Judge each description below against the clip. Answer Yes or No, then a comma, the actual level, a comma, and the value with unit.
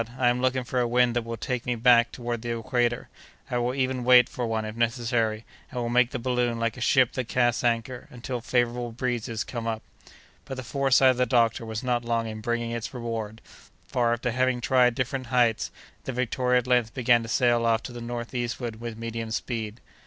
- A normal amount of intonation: No, narrow, 1.3 semitones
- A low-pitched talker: Yes, low, 120 Hz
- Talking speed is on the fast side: Yes, fast, 210 wpm